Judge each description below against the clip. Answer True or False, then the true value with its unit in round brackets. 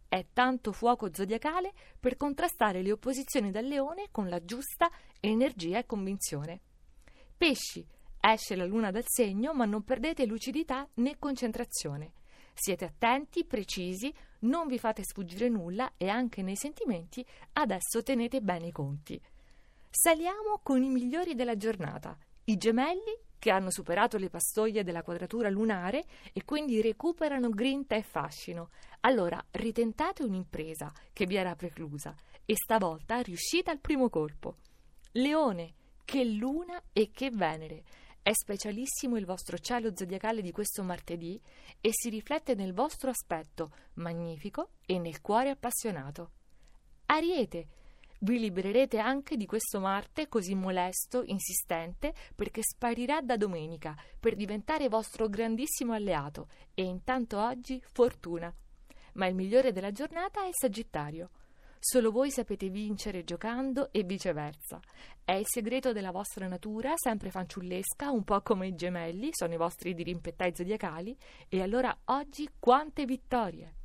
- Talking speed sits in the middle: True (135 wpm)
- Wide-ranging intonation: True (5.9 semitones)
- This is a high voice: True (220 Hz)